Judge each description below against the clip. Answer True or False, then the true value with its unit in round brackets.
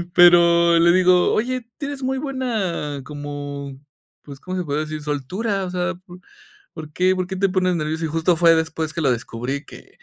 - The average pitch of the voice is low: False (170 Hz)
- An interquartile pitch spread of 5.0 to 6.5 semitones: False (3.7 semitones)